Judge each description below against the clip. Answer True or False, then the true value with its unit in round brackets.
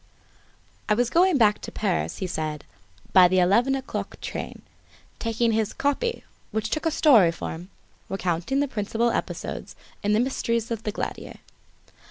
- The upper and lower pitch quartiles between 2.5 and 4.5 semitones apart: False (5.5 semitones)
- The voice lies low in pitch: False (220 Hz)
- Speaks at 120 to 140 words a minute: False (155 wpm)